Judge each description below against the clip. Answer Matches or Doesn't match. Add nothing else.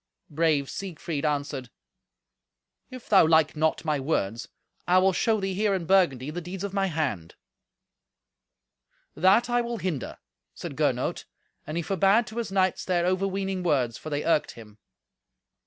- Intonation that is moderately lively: Matches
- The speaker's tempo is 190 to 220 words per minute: Doesn't match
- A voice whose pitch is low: Doesn't match